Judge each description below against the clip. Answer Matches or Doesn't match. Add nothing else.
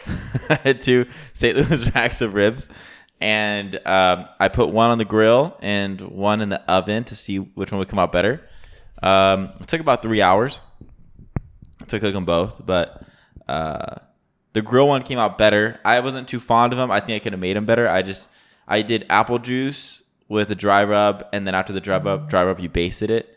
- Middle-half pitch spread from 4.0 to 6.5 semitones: Doesn't match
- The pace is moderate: Doesn't match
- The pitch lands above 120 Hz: Doesn't match